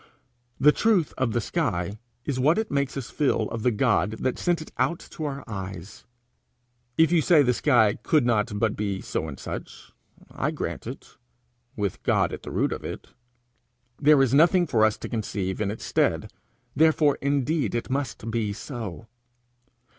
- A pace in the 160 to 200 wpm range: Yes, average, 175 wpm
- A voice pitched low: Yes, low, 125 Hz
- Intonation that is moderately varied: No, wide, 5.9 semitones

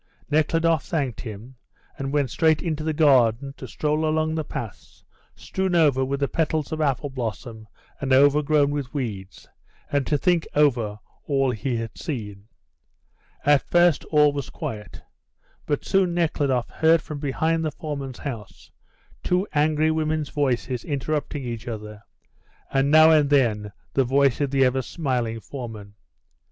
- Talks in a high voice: No, medium, 140 Hz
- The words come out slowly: No, average, 150 wpm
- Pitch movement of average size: Yes, average, 4.0 semitones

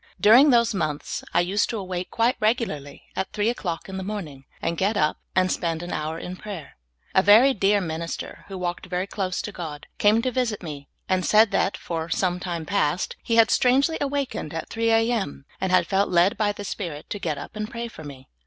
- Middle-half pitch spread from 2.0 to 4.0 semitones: No, average, 4.6 semitones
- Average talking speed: No, fast, 220 wpm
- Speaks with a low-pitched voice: No, high, 190 Hz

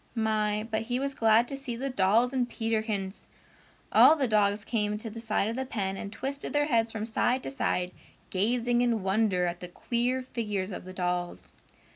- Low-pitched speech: No, high, 225 Hz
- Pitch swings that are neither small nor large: Yes, average, 3.3 semitones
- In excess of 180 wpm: Yes, average, 195 wpm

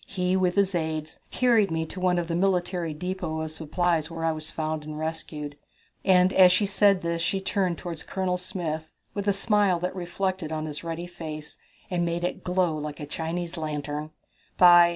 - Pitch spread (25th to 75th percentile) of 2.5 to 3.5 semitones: Yes, average, 2.8 semitones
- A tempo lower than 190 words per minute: No, average, 195 wpm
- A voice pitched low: No, medium, 175 Hz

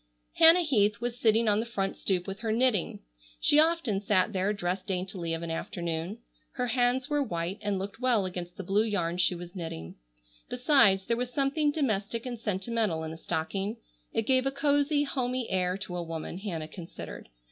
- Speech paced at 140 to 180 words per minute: No, average, 190 wpm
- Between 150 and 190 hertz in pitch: No, high, 205 Hz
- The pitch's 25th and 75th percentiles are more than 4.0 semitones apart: Yes, wide, 5.5 semitones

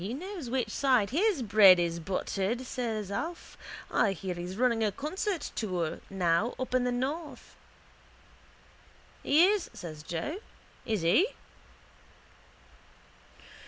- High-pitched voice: Yes, high, 230 Hz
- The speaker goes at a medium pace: No, slow, 125 wpm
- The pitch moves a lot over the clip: Yes, wide, 7.0 semitones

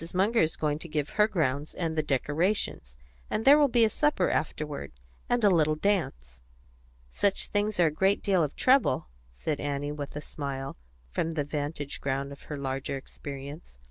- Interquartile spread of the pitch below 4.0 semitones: No, wide, 5.5 semitones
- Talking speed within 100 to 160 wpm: No, average, 180 wpm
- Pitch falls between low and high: Yes, medium, 155 Hz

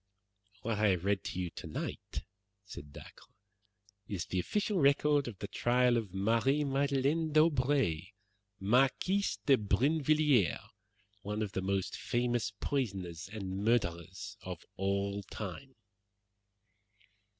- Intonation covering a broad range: Yes, wide, 6.1 semitones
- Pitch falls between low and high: No, low, 110 Hz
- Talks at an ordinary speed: No, slow, 115 wpm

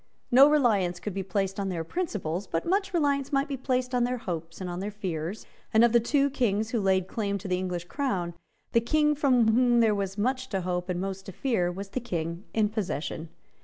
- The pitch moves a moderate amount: No, wide, 5.7 semitones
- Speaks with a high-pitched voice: Yes, high, 205 Hz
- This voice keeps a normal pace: No, fast, 225 wpm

